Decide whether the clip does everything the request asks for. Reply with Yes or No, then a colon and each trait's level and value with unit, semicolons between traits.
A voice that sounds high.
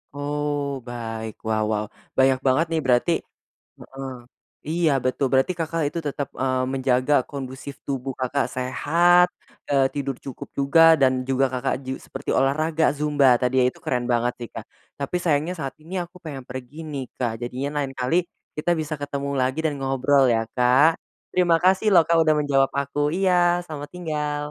No: medium, 140 Hz